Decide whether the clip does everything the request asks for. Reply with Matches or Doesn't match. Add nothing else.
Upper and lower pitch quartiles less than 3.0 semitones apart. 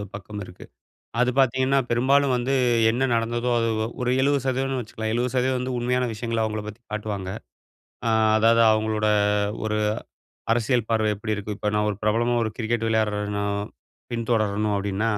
Matches